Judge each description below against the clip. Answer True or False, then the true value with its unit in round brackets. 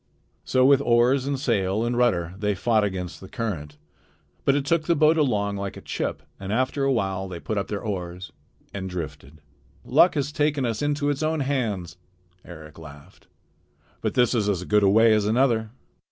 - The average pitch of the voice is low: True (110 Hz)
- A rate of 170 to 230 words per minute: True (190 wpm)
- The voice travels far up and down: True (6.3 semitones)